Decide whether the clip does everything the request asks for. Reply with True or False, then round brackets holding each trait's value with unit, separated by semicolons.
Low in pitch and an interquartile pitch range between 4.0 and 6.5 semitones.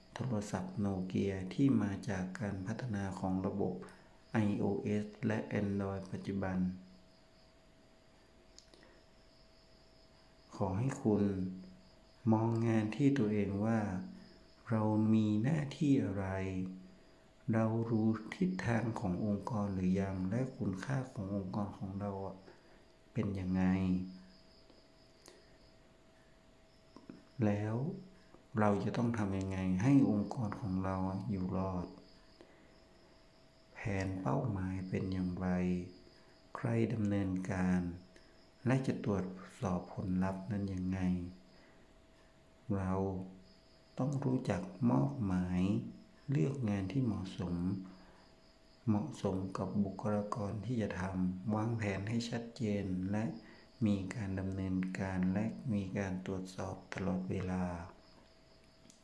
False (100 Hz; 2.7 semitones)